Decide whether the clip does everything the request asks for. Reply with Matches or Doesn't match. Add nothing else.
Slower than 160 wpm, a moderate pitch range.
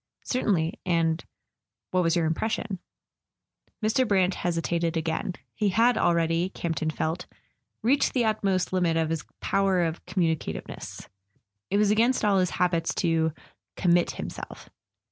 Matches